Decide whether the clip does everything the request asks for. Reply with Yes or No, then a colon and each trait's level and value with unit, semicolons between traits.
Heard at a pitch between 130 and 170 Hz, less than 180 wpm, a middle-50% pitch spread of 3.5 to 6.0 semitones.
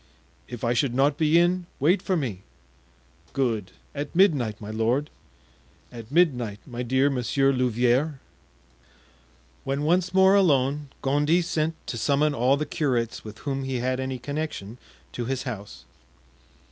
Yes: low, 135 Hz; average, 145 wpm; average, 3.9 semitones